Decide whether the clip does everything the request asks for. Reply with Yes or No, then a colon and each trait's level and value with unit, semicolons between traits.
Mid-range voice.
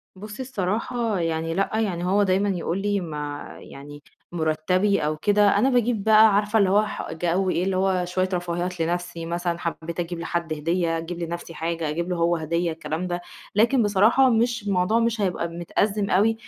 Yes: medium, 180 Hz